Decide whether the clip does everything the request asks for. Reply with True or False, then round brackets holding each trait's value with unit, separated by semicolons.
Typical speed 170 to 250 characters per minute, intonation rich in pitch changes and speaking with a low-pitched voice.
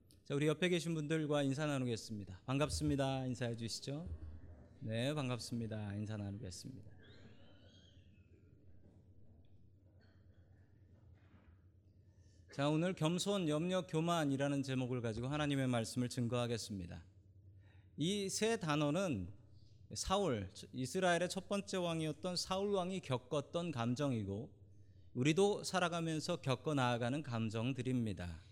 False (265 characters per minute; 7.3 semitones; 120 Hz)